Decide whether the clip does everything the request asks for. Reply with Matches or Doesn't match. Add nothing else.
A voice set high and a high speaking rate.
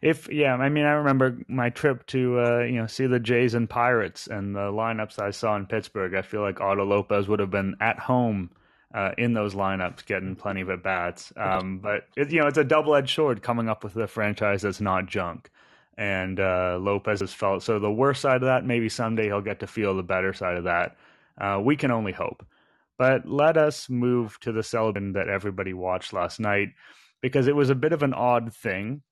Doesn't match